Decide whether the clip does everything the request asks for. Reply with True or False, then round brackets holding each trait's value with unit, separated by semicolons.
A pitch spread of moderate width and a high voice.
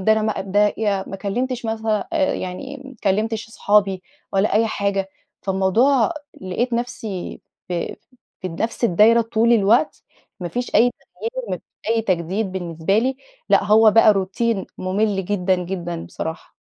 True (3.3 semitones; 210 Hz)